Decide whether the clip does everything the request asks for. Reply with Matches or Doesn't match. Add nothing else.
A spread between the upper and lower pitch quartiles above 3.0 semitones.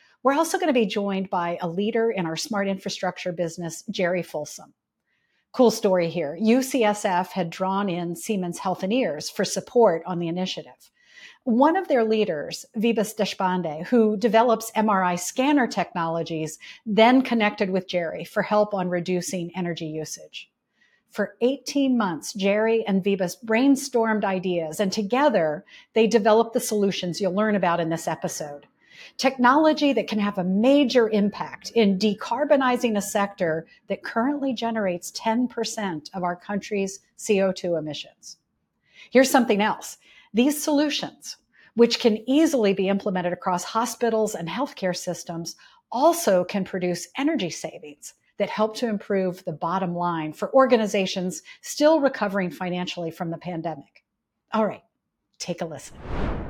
Matches